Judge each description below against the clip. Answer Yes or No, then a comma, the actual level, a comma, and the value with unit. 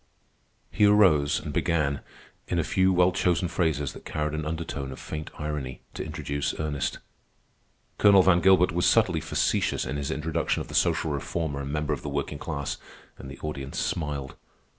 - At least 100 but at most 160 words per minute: No, average, 175 wpm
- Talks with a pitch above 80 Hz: No, very low, 75 Hz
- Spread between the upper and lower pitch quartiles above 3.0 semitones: Yes, average, 3.5 semitones